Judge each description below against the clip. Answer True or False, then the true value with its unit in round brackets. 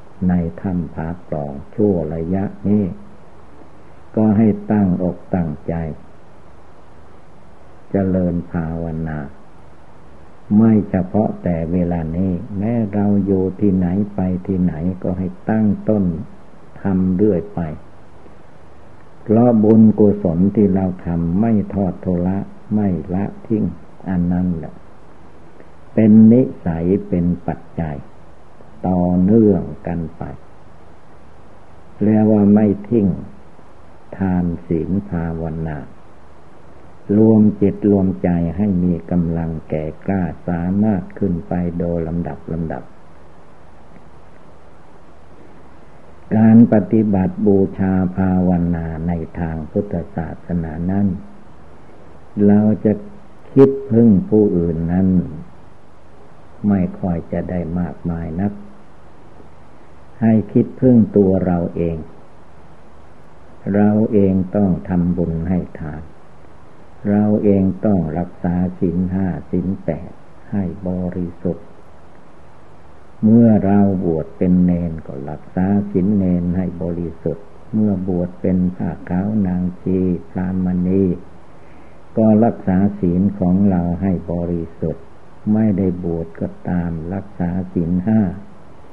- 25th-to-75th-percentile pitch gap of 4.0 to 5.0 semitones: False (3.1 semitones)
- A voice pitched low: True (90 Hz)